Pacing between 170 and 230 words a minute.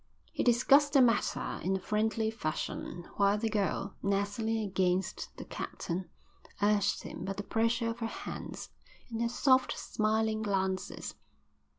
No: average, 145 wpm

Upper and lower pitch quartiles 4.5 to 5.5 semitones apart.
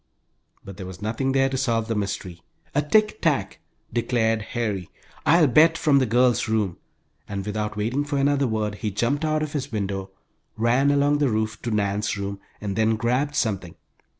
Yes: average, 5.0 semitones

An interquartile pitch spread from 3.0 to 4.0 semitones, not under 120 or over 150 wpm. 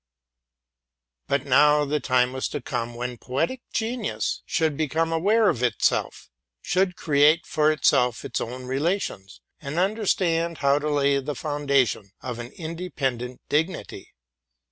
No: average, 4.4 semitones; slow, 135 wpm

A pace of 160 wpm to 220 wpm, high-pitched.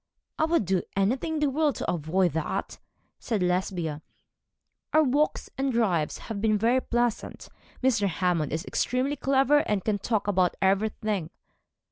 No: average, 150 wpm; high, 210 Hz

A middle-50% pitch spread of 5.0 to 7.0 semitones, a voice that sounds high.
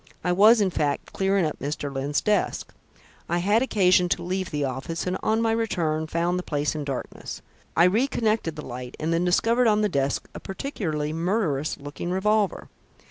No: wide, 5.6 semitones; medium, 175 Hz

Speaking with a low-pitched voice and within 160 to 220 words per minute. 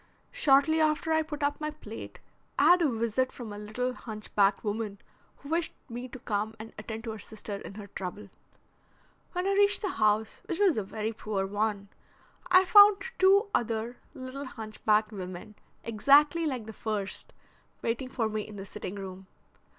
No: high, 225 Hz; average, 180 wpm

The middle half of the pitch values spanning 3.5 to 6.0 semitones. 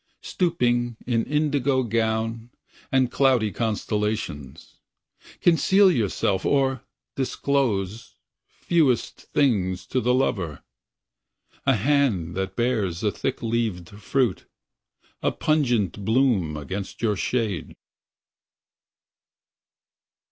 Yes: average, 5.1 semitones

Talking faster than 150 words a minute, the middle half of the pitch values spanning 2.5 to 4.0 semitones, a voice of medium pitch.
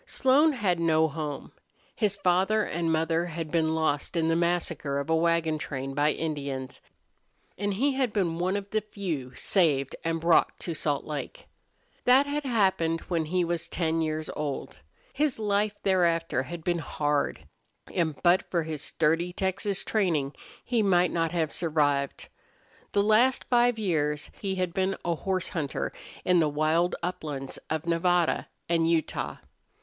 Yes: average, 160 wpm; average, 3.5 semitones; medium, 170 Hz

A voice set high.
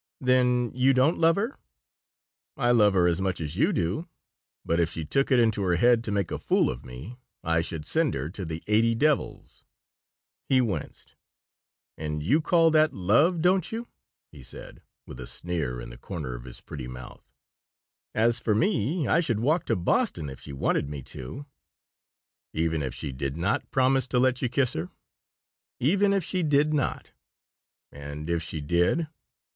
No: low, 105 Hz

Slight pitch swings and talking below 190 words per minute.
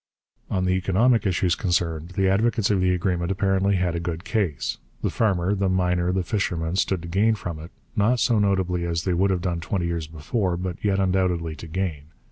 No: narrow, 2.3 semitones; fast, 205 wpm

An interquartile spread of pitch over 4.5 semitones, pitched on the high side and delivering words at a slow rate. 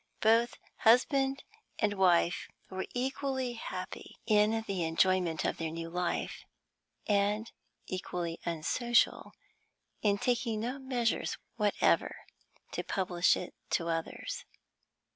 Yes: average, 5.2 semitones; high, 205 Hz; slow, 105 wpm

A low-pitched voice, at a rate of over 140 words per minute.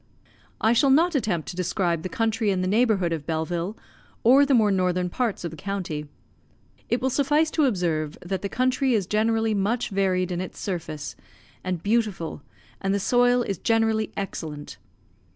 No: high, 200 Hz; average, 170 wpm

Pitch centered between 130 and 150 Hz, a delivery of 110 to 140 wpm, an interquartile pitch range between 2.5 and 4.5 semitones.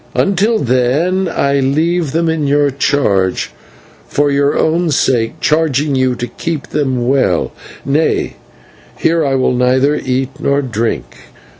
Yes: medium, 140 Hz; slow, 135 wpm; average, 3.5 semitones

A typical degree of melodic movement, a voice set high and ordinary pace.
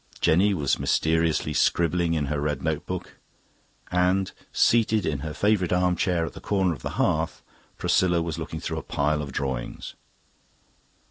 No: average, 3.4 semitones; very low, 85 Hz; average, 155 wpm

